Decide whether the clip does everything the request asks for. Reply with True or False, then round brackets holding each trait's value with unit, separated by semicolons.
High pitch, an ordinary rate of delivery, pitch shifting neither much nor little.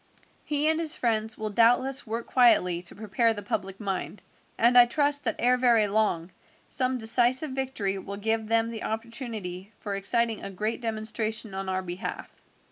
True (225 Hz; 170 wpm; 3.4 semitones)